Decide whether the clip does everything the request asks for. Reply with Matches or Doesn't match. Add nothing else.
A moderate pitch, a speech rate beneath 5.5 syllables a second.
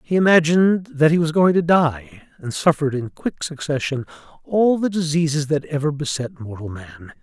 Matches